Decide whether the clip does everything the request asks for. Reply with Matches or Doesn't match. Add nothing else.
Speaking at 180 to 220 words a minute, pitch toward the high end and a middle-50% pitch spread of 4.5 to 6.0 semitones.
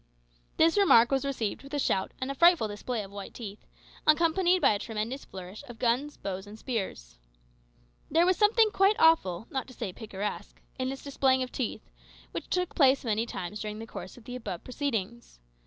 Matches